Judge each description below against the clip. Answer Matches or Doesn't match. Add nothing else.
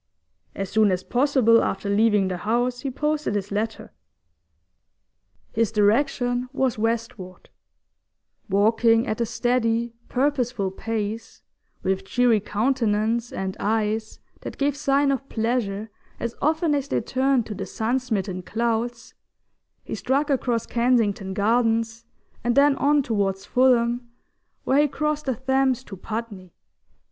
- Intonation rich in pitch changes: Doesn't match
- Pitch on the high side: Matches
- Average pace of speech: Doesn't match